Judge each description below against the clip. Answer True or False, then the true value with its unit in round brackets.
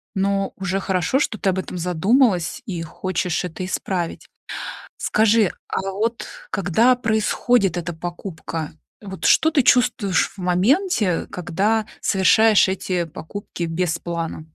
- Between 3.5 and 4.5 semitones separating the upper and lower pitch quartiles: True (3.9 semitones)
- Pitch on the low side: False (190 Hz)